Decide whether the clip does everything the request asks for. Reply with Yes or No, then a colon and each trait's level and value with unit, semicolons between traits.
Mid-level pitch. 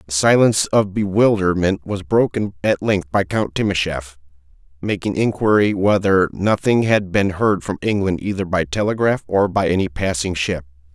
No: very low, 95 Hz